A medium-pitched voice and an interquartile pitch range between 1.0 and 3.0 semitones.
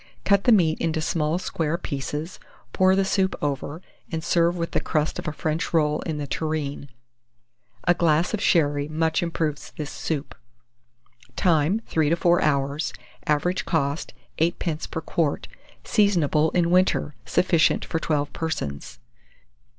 Yes: medium, 160 Hz; narrow, 2.6 semitones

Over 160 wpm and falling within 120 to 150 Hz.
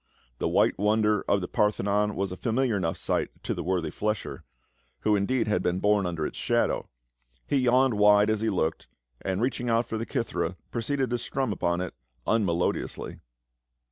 No: average, 180 wpm; low, 105 Hz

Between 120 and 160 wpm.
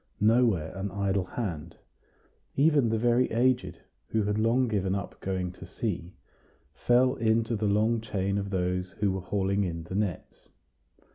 Yes: average, 155 wpm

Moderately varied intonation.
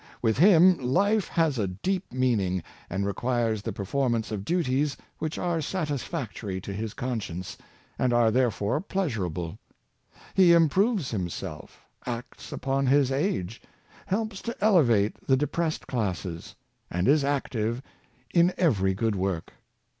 No: wide, 8.0 semitones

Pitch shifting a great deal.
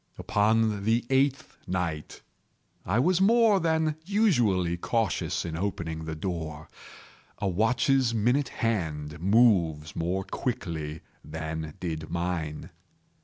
Yes: wide, 7.3 semitones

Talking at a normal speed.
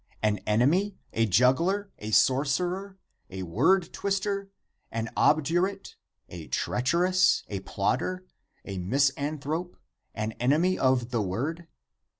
No: slow, 115 wpm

